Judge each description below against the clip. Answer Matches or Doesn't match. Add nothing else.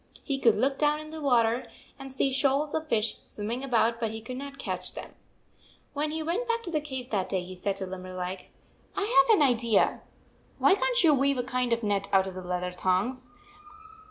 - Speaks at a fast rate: Matches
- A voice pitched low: Doesn't match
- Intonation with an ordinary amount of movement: Doesn't match